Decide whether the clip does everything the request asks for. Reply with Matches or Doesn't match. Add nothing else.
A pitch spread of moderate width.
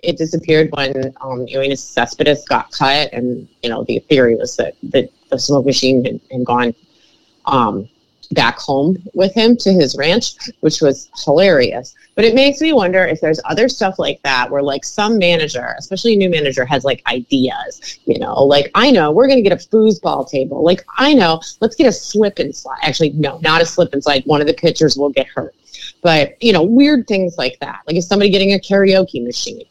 Doesn't match